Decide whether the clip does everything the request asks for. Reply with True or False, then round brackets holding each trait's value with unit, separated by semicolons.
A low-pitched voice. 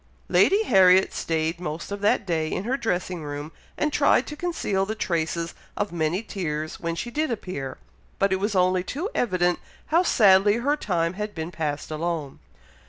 False (185 Hz)